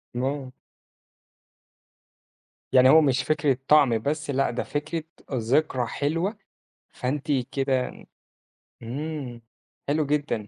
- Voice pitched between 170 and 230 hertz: No, medium, 140 Hz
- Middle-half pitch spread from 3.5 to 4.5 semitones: No, average, 3.0 semitones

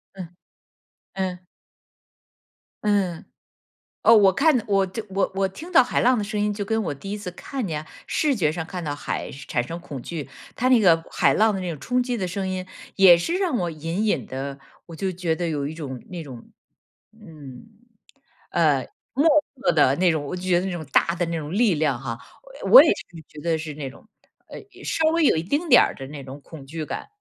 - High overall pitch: No, medium, 175 Hz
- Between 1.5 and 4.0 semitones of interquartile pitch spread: No, average, 5.3 semitones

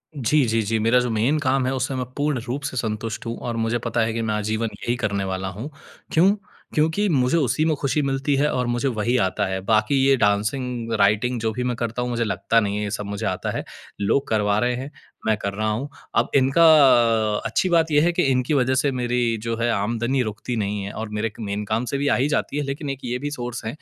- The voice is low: Yes, low, 120 Hz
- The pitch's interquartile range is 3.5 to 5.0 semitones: Yes, average, 4.0 semitones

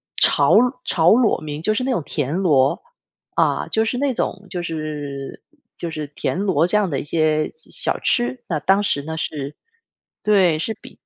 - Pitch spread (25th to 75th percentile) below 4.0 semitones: No, wide, 5.6 semitones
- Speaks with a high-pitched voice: No, medium, 165 Hz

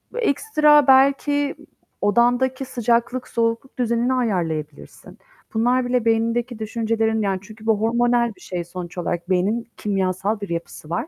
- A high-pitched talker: Yes, high, 230 Hz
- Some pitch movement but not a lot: Yes, average, 4.3 semitones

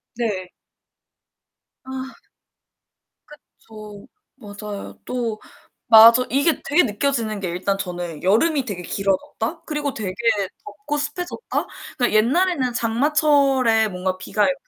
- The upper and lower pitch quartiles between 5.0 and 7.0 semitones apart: Yes, wide, 5.4 semitones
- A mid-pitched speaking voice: No, high, 230 Hz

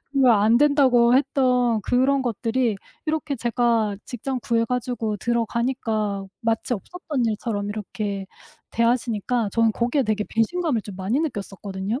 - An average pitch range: Yes, average, 3.1 semitones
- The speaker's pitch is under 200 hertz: No, high, 235 Hz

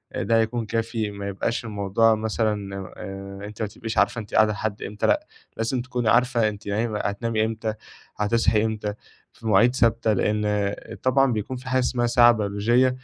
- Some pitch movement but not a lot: No, narrow, 2.3 semitones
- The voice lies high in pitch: No, low, 110 Hz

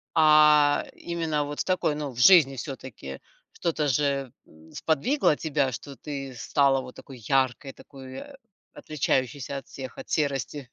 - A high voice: No, medium, 140 Hz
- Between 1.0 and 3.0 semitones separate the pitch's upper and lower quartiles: Yes, narrow, 2.5 semitones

